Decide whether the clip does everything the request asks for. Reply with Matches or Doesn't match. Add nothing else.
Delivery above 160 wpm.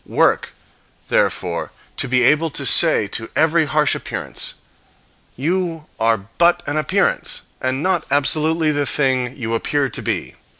Doesn't match